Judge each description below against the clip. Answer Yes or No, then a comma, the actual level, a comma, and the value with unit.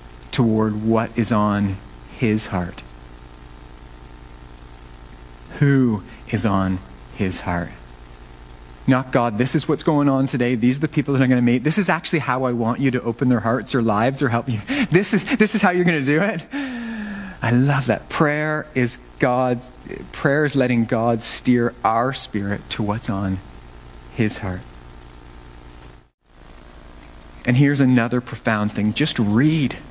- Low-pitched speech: Yes, low, 115 Hz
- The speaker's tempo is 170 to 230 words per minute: No, average, 160 wpm